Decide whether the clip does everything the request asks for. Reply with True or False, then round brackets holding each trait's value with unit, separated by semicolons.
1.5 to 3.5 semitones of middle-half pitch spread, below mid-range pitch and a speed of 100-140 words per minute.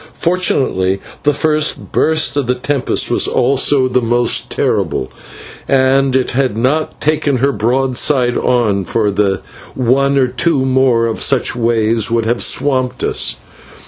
True (2.9 semitones; 130 Hz; 135 wpm)